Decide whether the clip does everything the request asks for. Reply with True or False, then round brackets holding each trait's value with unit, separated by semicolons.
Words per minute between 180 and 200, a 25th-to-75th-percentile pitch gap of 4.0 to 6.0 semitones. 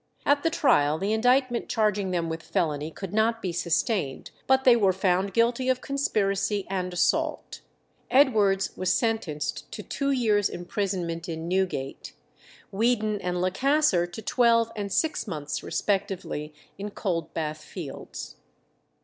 False (135 wpm; 4.8 semitones)